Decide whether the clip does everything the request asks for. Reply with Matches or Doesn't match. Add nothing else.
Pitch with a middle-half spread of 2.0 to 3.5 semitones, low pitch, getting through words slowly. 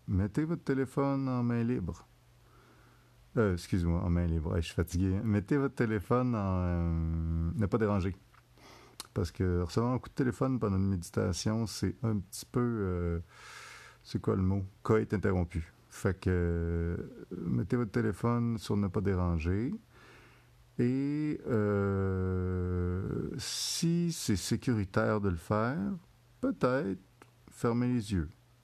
Doesn't match